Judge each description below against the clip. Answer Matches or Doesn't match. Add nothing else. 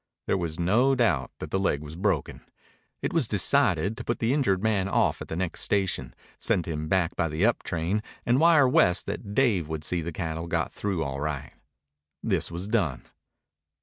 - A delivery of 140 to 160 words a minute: Doesn't match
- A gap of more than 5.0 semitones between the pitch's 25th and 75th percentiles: Matches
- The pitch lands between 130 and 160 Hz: Doesn't match